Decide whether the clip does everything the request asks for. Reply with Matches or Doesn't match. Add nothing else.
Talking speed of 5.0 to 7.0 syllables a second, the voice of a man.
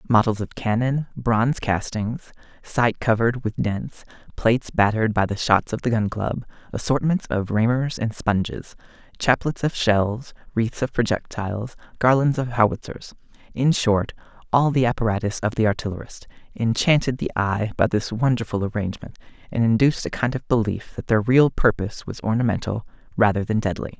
Matches